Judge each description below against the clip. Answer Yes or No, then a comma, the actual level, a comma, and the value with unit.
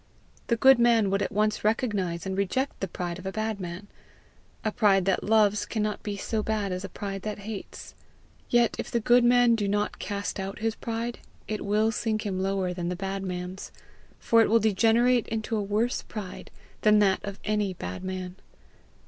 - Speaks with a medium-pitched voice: No, high, 210 Hz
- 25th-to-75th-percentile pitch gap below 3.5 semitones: Yes, narrow, 2.6 semitones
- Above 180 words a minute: Yes, average, 195 wpm